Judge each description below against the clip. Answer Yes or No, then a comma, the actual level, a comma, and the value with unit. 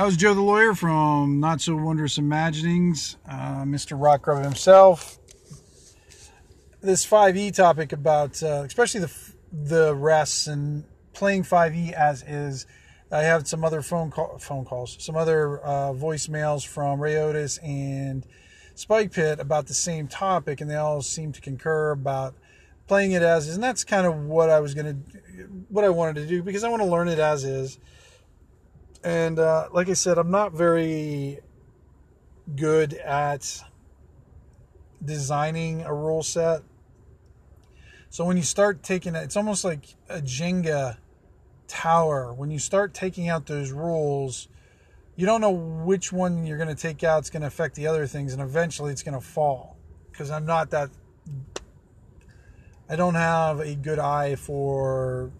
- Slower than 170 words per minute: Yes, average, 160 wpm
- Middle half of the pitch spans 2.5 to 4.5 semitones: Yes, average, 3.4 semitones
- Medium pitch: Yes, medium, 150 Hz